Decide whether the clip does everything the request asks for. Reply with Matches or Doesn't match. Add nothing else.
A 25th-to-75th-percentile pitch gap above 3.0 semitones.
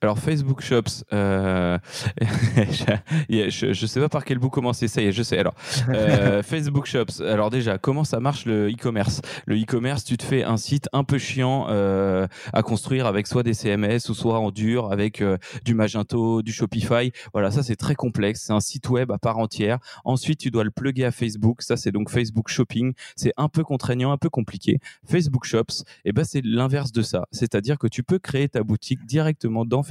Matches